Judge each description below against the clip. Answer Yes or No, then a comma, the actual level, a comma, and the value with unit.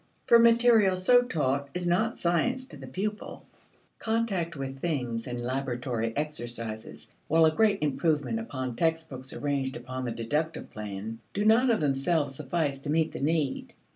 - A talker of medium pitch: Yes, medium, 150 Hz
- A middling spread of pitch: No, wide, 5.8 semitones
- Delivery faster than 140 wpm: Yes, average, 155 wpm